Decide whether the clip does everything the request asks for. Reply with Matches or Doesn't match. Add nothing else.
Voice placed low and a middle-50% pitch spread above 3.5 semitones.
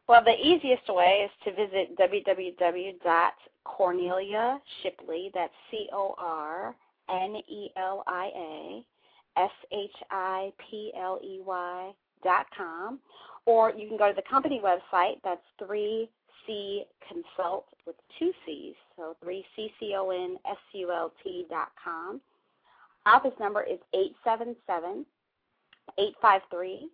Doesn't match